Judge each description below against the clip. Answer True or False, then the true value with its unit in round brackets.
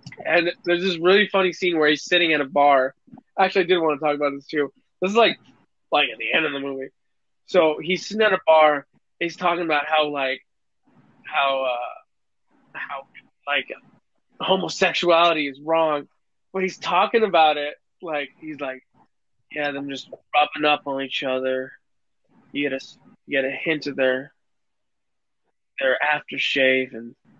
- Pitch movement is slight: False (4.1 semitones)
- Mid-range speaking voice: True (150 Hz)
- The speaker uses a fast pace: False (170 wpm)